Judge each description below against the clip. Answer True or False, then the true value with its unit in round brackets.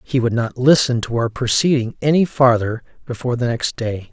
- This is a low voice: True (125 Hz)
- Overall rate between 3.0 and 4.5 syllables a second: False (5.3 syllables/s)